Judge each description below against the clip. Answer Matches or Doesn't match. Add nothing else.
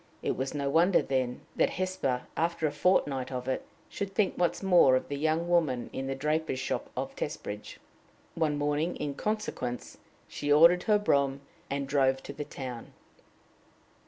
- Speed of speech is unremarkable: Matches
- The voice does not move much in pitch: Doesn't match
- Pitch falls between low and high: Matches